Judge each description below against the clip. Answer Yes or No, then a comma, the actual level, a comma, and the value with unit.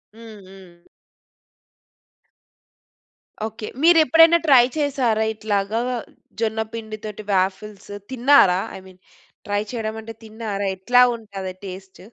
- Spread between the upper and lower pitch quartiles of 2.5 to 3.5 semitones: Yes, average, 2.8 semitones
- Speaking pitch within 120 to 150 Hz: No, high, 215 Hz